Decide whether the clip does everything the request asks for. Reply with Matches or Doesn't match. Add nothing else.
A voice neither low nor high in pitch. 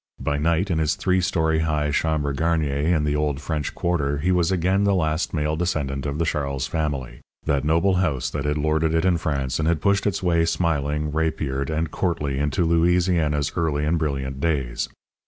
Doesn't match